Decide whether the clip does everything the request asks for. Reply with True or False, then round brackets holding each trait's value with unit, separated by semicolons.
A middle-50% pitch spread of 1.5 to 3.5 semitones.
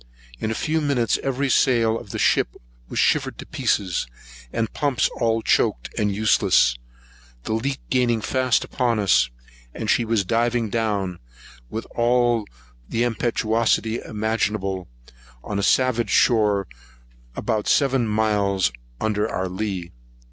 True (2.7 semitones)